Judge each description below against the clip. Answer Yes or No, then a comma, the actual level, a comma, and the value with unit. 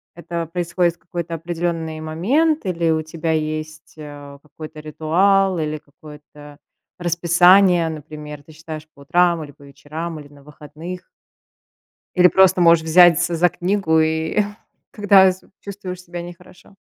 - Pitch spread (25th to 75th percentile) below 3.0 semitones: Yes, narrow, 2.4 semitones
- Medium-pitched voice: Yes, medium, 165 Hz